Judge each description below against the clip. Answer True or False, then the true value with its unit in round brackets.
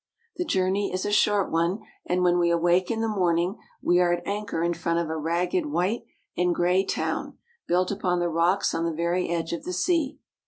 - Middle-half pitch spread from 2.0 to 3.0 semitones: True (2.7 semitones)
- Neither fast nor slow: False (210 wpm)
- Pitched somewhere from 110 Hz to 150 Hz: False (180 Hz)